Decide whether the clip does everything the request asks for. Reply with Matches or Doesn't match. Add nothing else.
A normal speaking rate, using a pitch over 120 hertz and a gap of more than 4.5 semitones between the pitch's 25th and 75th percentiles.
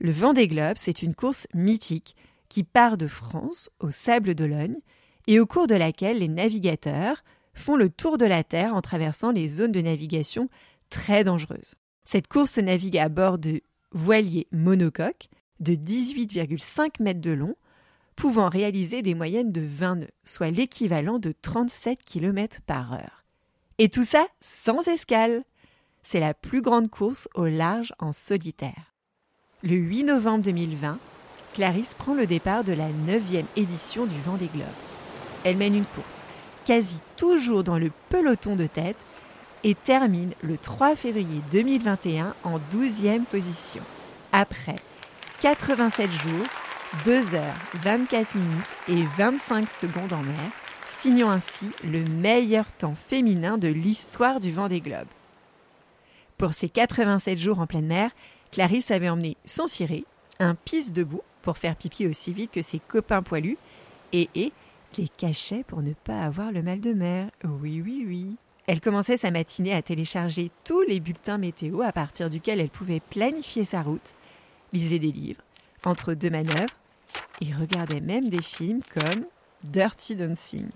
Matches